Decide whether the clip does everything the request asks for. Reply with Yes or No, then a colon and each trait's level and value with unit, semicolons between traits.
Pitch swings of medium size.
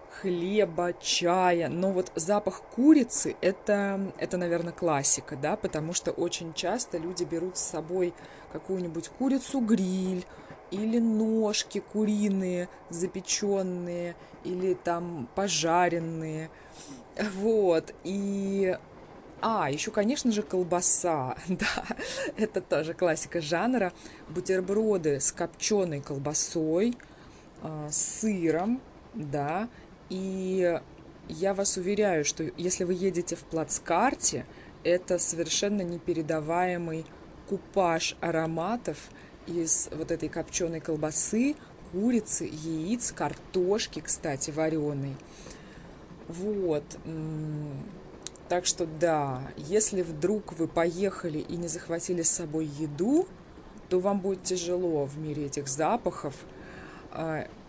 Yes: average, 3.3 semitones